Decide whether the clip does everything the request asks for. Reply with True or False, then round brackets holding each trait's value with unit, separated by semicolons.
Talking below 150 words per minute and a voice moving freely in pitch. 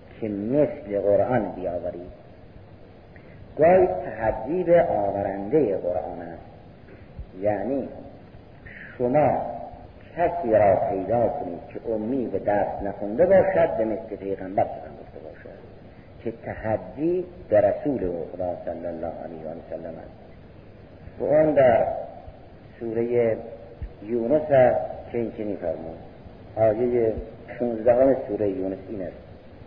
False (105 wpm; 4.0 semitones)